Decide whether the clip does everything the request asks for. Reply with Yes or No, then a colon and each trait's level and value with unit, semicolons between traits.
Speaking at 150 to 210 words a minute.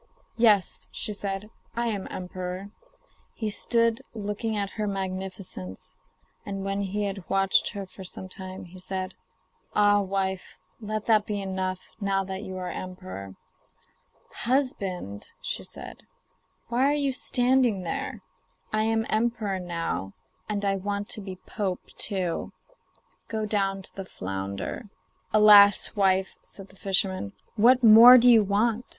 No: average, 140 wpm